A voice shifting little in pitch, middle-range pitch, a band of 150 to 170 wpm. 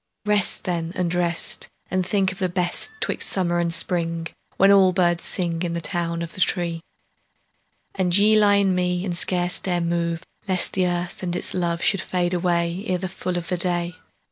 No: narrow, 1.5 semitones; medium, 175 Hz; average, 195 wpm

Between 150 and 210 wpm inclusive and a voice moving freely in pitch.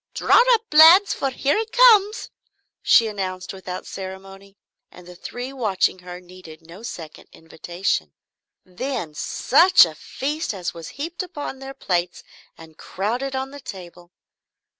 No: average, 140 wpm; wide, 7.5 semitones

